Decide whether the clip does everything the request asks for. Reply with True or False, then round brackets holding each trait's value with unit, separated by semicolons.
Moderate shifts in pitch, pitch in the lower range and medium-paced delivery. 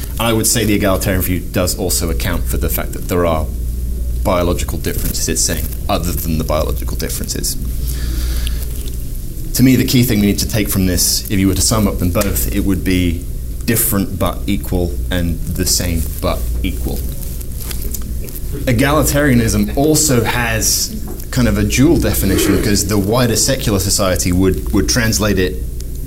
False (6.4 semitones; 90 Hz; 165 wpm)